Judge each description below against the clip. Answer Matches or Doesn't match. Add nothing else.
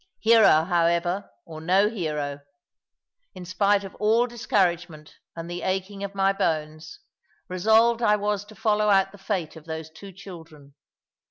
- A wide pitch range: Doesn't match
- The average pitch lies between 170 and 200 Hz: Matches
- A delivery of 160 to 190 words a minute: Doesn't match